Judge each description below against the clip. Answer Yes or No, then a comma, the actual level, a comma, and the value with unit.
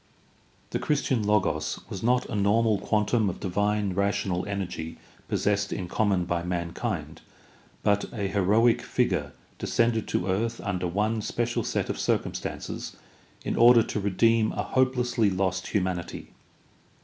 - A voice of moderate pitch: No, low, 105 Hz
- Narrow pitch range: No, average, 3.3 semitones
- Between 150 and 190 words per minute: No, slow, 135 wpm